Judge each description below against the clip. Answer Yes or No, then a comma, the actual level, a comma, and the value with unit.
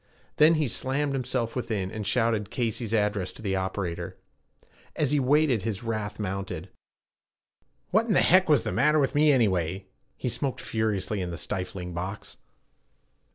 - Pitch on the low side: Yes, low, 110 Hz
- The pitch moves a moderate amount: No, wide, 5.8 semitones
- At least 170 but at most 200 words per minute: No, average, 155 wpm